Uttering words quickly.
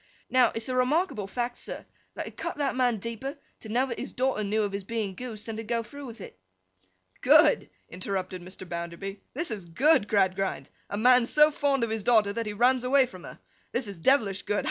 Yes: fast, 215 wpm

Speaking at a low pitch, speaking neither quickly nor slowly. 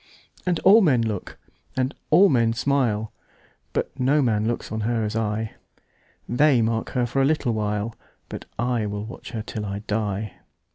Yes: low, 115 Hz; average, 155 wpm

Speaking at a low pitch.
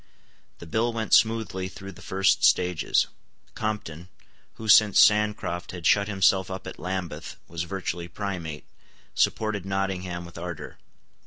Yes: very low, 95 Hz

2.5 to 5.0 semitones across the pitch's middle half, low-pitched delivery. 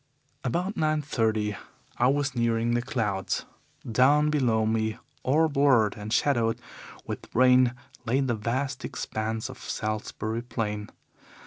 Yes: average, 3.7 semitones; low, 120 Hz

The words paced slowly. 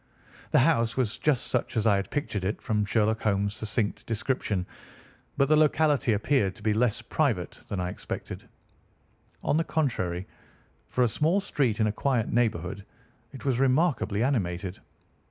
No: average, 160 wpm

